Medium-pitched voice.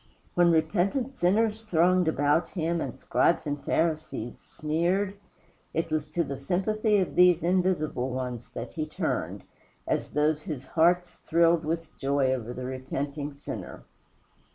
Yes: medium, 160 Hz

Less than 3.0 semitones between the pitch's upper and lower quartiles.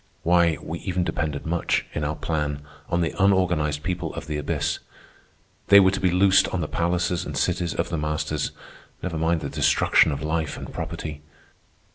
Yes: narrow, 2.6 semitones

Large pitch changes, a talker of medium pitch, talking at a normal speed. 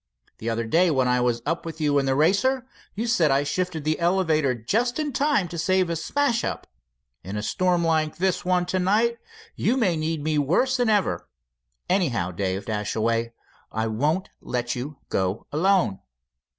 Yes: wide, 7.3 semitones; medium, 160 Hz; average, 180 wpm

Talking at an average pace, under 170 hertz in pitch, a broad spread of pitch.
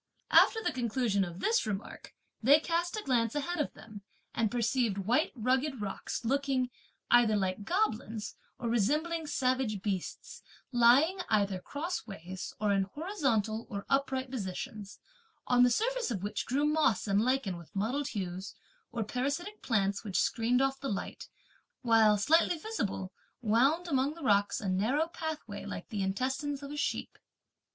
No: average, 155 wpm; high, 245 Hz; wide, 5.8 semitones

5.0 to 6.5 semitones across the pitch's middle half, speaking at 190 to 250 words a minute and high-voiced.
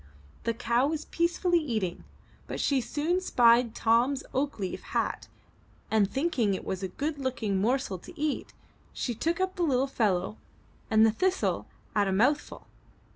No: wide, 5.6 semitones; average, 155 wpm; very high, 250 Hz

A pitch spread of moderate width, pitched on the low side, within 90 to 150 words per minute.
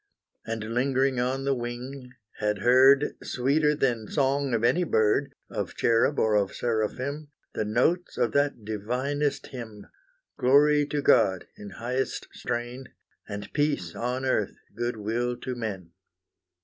Yes: average, 3.8 semitones; low, 125 Hz; slow, 135 wpm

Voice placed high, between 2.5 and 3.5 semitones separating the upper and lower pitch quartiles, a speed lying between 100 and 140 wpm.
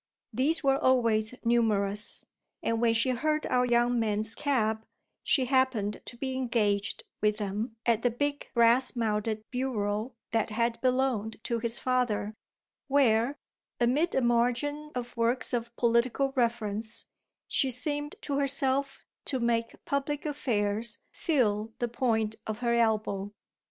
Yes: high, 235 Hz; average, 3.0 semitones; slow, 135 wpm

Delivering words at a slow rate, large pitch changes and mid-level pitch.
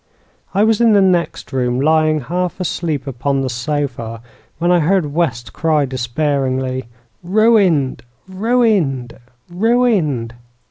Yes: slow, 120 wpm; wide, 6.2 semitones; medium, 155 Hz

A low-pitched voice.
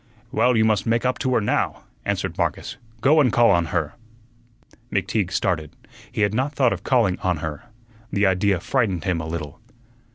Yes: low, 100 Hz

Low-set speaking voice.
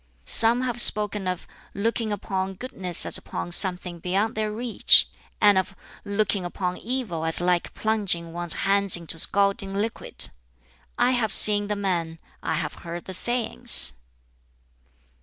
No: high, 195 Hz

